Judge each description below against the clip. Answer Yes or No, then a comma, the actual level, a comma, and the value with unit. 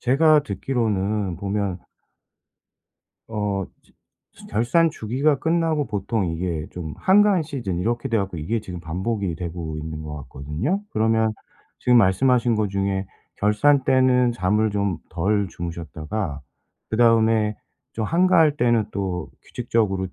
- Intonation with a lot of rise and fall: No, average, 5.0 semitones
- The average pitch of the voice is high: No, low, 105 Hz